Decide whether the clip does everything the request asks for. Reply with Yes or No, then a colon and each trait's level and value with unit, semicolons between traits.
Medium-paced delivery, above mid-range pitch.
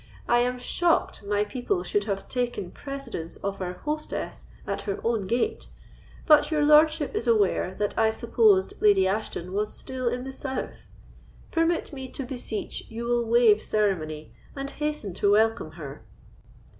Yes: average, 155 wpm; high, 230 Hz